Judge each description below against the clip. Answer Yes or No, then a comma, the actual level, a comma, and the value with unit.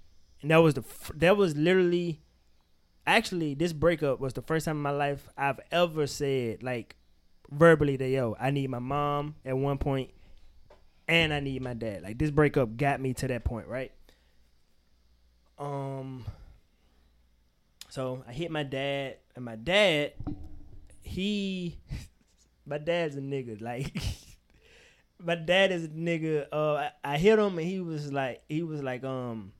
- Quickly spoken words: No, average, 160 wpm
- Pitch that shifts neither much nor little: No, wide, 6.6 semitones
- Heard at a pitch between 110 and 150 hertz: Yes, medium, 140 Hz